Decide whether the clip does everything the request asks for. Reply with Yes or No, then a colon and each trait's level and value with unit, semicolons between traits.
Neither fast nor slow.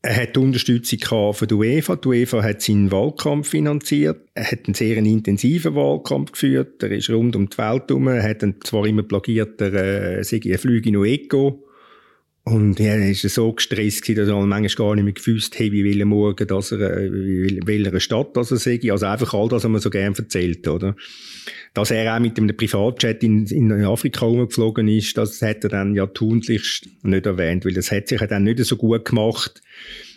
No: fast, 205 wpm